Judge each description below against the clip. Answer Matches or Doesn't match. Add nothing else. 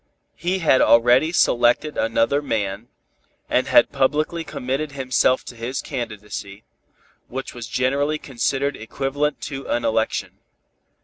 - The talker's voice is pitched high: Doesn't match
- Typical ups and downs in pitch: Matches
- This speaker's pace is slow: Matches